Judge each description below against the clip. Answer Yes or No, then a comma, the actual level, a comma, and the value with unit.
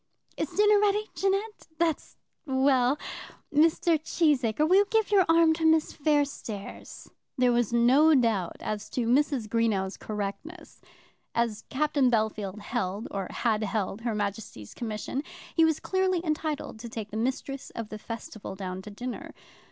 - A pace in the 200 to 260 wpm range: No, average, 150 wpm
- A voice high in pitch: Yes, very high, 250 Hz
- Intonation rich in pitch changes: Yes, wide, 6.8 semitones